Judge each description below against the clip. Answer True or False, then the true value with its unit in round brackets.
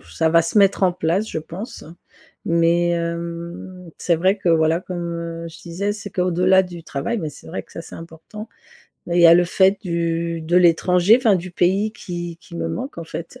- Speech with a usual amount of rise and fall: False (1.9 semitones)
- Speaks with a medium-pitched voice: True (175 Hz)